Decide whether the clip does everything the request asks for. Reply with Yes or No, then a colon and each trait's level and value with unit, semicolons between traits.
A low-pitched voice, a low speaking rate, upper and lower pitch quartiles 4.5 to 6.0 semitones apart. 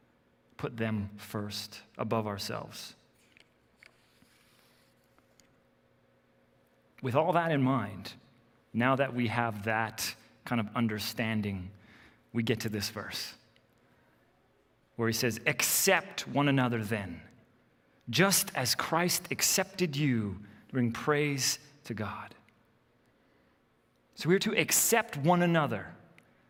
Yes: low, 115 Hz; slow, 100 wpm; wide, 5.6 semitones